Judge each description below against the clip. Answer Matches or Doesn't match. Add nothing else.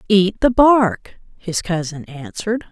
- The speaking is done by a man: Doesn't match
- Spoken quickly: Doesn't match